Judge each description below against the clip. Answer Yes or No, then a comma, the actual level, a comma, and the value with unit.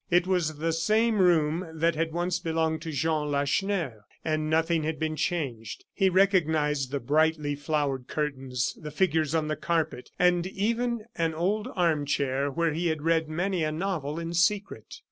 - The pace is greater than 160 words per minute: Yes, average, 170 wpm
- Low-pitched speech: No, medium, 160 Hz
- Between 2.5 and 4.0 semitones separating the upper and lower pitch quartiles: Yes, average, 2.8 semitones